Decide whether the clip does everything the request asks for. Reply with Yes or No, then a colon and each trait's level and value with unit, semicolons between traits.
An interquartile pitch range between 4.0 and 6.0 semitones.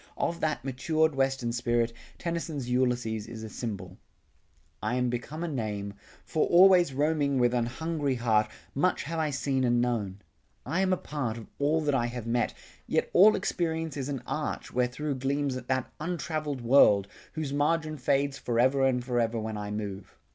Yes: average, 4.4 semitones